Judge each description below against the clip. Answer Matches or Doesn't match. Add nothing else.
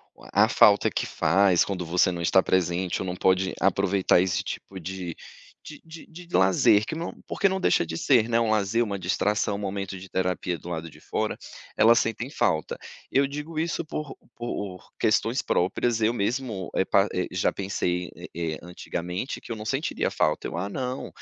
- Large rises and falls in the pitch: Doesn't match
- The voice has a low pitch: Matches